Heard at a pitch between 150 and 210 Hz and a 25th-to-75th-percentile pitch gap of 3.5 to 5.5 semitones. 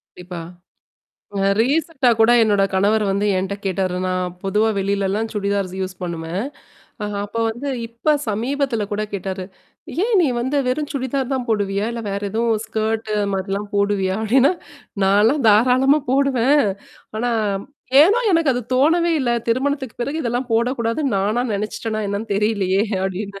No: high, 220 Hz; average, 4.5 semitones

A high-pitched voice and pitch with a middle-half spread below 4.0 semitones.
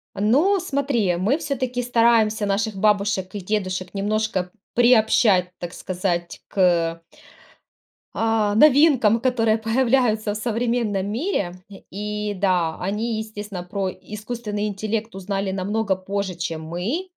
Yes: high, 210 Hz; average, 3.5 semitones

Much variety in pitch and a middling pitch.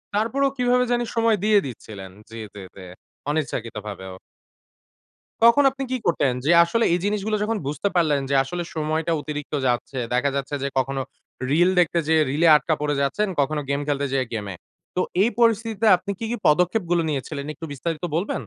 Yes: wide, 7.2 semitones; medium, 155 Hz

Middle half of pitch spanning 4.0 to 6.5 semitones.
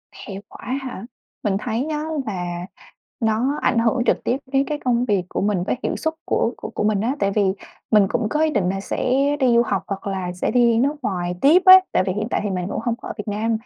Yes: average, 4.4 semitones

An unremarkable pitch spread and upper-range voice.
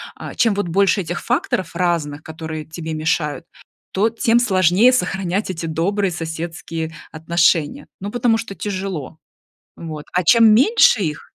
No: average, 4.1 semitones; medium, 175 Hz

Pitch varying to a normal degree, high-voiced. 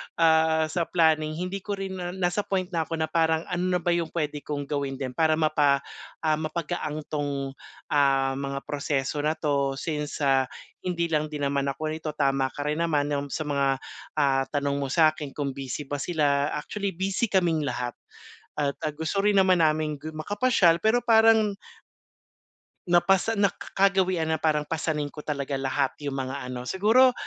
No: average, 3.7 semitones; medium, 155 Hz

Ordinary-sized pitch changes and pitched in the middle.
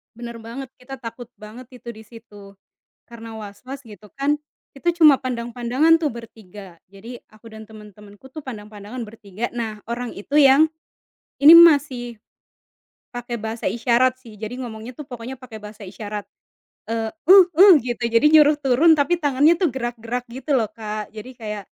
No: average, 3.6 semitones; high, 235 Hz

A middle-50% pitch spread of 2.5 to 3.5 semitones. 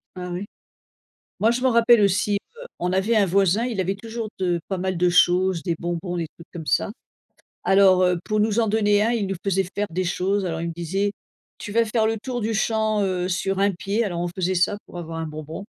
Yes: average, 3.2 semitones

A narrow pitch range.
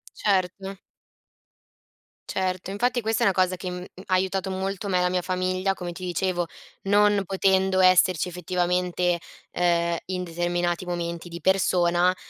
Yes: narrow, 1.4 semitones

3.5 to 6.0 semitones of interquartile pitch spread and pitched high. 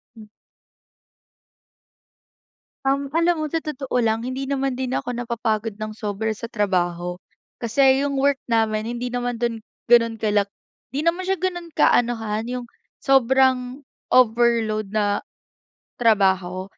Yes: average, 3.8 semitones; high, 235 Hz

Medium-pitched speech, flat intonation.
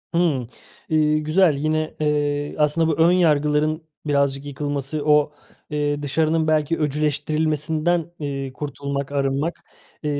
Yes: medium, 150 Hz; narrow, 1.5 semitones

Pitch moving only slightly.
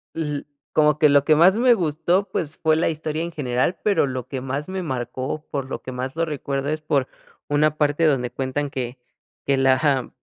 No: average, 3.1 semitones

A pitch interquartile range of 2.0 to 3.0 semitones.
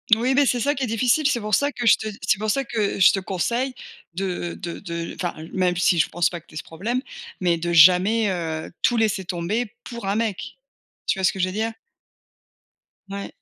No: average, 5.0 semitones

